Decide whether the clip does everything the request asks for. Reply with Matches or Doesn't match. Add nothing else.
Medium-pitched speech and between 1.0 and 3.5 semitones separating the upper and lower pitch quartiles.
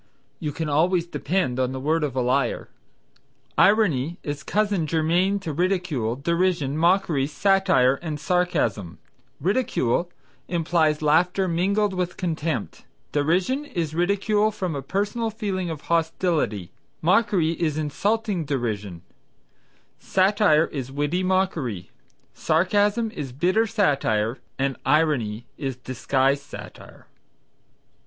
Doesn't match